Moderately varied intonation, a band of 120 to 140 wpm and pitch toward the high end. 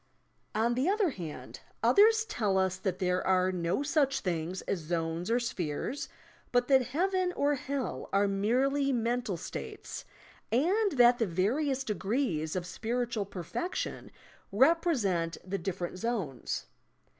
No: wide, 7.0 semitones; slow, 135 wpm; high, 225 Hz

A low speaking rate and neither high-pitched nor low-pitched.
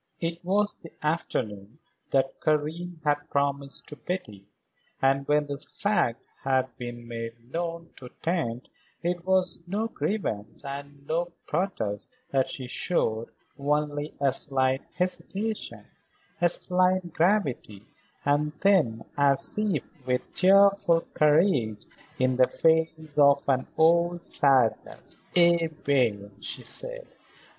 Yes: slow, 120 wpm; medium, 150 Hz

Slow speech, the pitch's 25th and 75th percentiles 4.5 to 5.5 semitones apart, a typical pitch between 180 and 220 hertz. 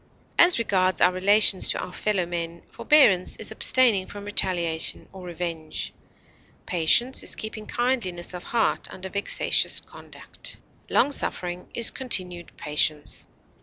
No: slow, 130 wpm; average, 3.8 semitones; medium, 185 Hz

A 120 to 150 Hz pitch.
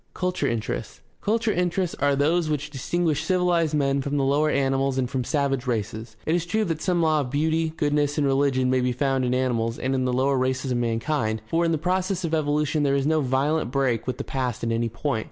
Yes: medium, 140 Hz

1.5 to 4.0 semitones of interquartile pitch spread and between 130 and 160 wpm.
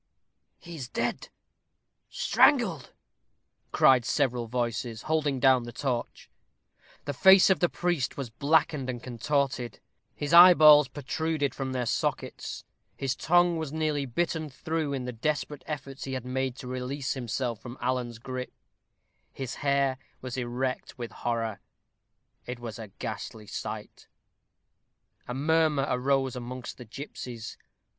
Yes: average, 3.3 semitones; slow, 135 wpm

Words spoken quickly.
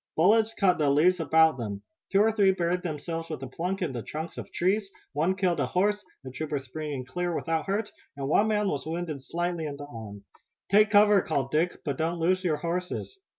Yes: fast, 210 wpm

